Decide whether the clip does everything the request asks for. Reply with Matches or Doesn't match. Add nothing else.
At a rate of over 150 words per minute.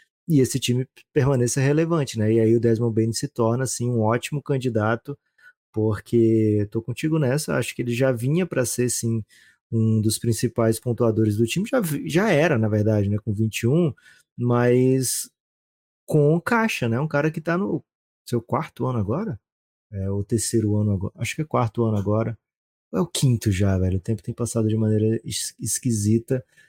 Matches